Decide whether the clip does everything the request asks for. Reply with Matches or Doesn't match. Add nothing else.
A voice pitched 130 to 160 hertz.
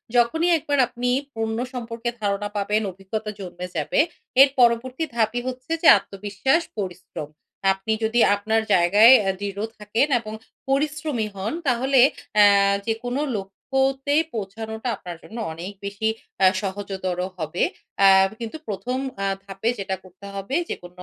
Doesn't match